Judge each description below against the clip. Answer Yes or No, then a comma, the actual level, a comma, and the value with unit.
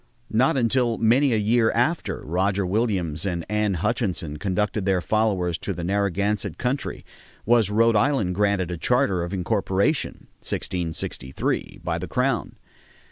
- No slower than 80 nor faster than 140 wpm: Yes, slow, 135 wpm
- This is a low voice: Yes, low, 100 Hz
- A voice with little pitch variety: No, average, 4.2 semitones